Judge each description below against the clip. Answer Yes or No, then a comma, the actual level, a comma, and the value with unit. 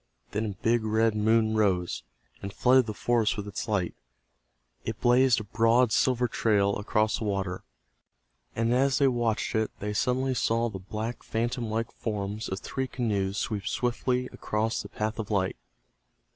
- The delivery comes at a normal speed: Yes, average, 165 wpm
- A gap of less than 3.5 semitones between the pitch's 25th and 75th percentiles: Yes, narrow, 2.6 semitones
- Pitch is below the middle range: Yes, low, 110 Hz